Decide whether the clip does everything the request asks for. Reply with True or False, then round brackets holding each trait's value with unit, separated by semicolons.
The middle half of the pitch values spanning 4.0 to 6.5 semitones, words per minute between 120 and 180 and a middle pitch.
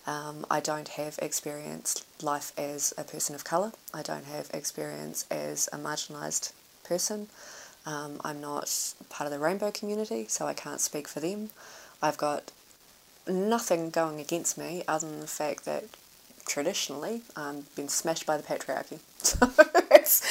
True (4.4 semitones; 150 wpm; 155 Hz)